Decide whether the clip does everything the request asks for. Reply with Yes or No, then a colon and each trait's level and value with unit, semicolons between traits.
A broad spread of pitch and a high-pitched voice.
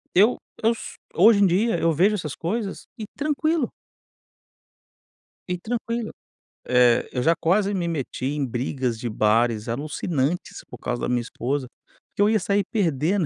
No: wide, 8.5 semitones; medium, 170 Hz